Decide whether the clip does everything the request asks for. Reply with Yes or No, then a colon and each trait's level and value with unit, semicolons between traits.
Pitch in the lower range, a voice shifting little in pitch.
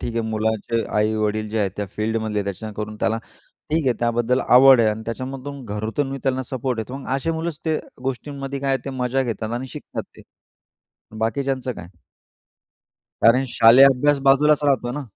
No: low, 125 Hz; average, 3.6 semitones